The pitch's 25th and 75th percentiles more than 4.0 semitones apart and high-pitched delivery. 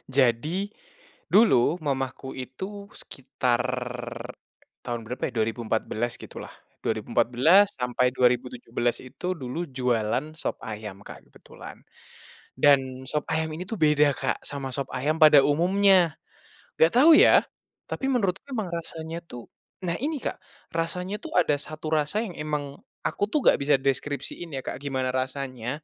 No: average, 4.7 semitones; medium, 140 Hz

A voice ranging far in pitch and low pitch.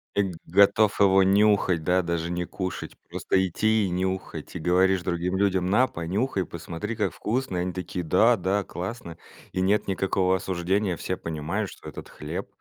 No: narrow, 2.4 semitones; very low, 95 Hz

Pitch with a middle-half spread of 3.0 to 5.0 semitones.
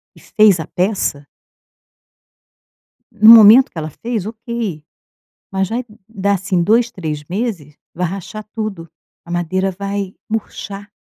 Yes: average, 3.9 semitones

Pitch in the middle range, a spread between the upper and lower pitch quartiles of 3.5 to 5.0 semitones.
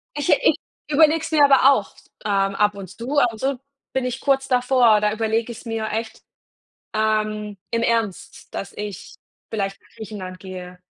No: high, 220 Hz; average, 4.0 semitones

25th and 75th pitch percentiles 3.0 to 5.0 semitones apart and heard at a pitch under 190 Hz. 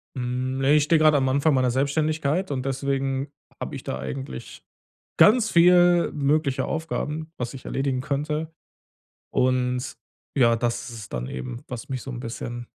Yes: average, 3.7 semitones; low, 135 Hz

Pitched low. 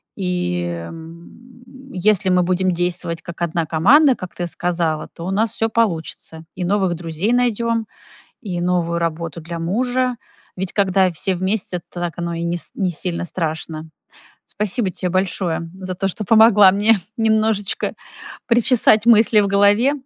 No: medium, 185 Hz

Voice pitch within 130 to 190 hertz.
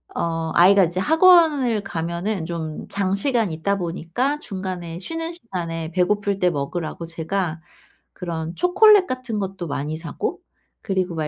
Yes: medium, 185 Hz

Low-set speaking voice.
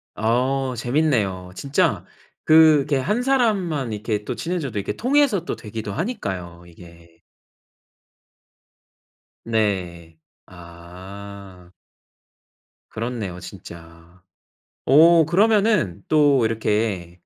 Yes: low, 110 Hz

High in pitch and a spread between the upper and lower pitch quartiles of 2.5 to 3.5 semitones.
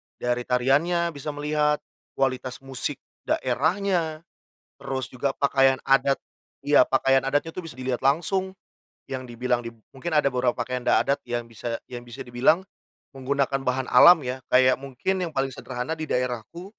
No: low, 135 Hz; average, 3.0 semitones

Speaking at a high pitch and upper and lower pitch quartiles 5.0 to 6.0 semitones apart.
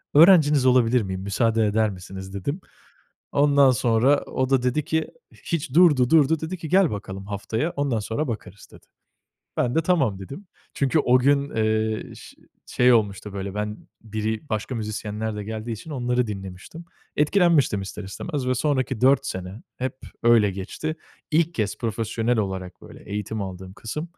No: low, 115 Hz; wide, 5.4 semitones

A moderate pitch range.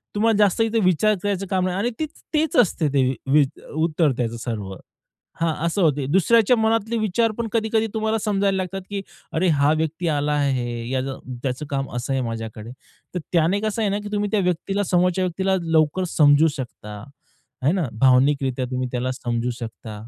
No: wide, 7.4 semitones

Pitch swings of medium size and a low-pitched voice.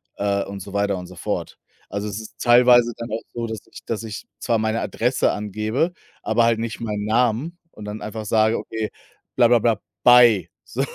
No: narrow, 2.2 semitones; low, 110 Hz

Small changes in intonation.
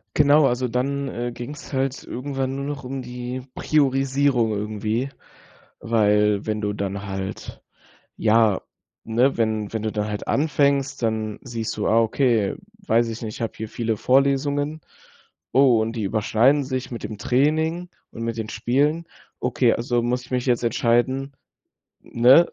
No: average, 3.6 semitones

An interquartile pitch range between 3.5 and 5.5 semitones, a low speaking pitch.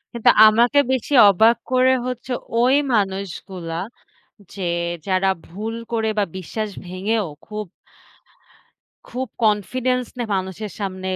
No: average, 3.8 semitones; high, 215 Hz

